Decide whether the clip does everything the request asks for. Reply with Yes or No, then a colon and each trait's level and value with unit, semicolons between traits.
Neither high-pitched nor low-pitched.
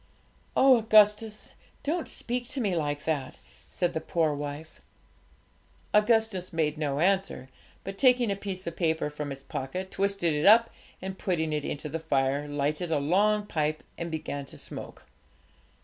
Yes: medium, 170 Hz